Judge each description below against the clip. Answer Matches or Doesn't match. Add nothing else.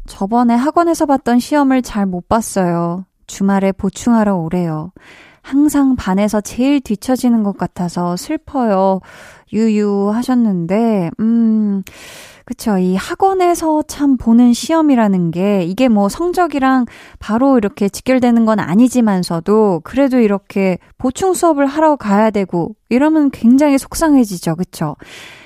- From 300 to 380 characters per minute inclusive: Doesn't match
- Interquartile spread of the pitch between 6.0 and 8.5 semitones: Doesn't match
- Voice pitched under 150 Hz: Doesn't match